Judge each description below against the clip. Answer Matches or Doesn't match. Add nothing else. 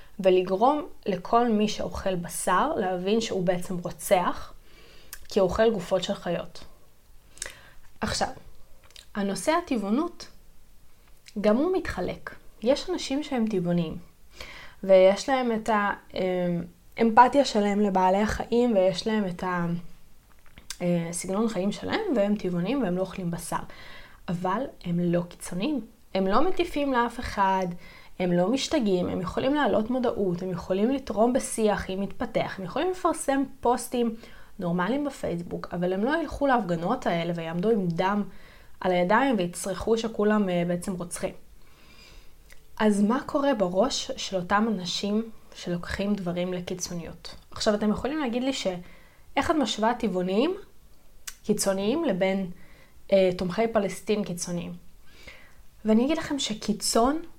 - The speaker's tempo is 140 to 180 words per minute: Doesn't match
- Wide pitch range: Doesn't match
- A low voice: Doesn't match